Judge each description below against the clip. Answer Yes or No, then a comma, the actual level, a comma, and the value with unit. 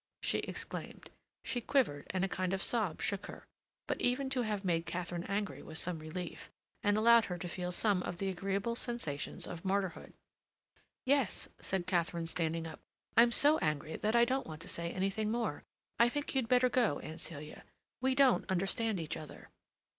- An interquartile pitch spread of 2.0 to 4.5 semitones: No, wide, 5.6 semitones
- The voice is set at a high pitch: Yes, high, 195 Hz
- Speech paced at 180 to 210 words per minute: Yes, average, 185 wpm